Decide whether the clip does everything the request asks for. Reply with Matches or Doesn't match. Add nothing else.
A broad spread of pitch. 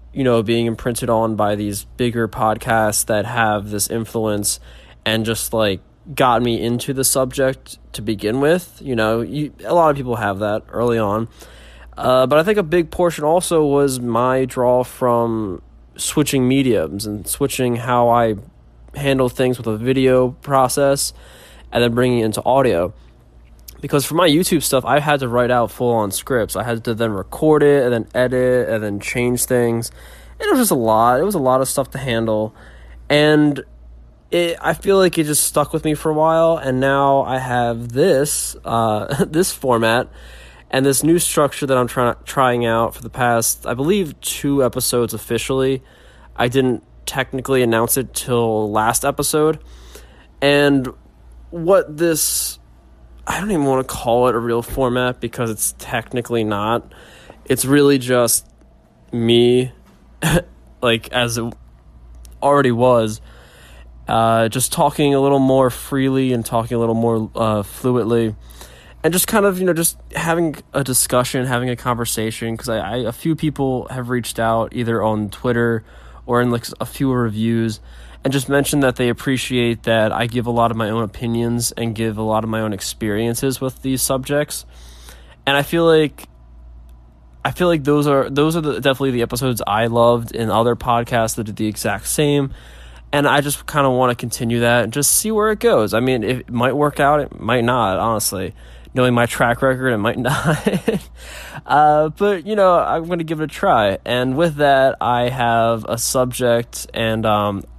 Doesn't match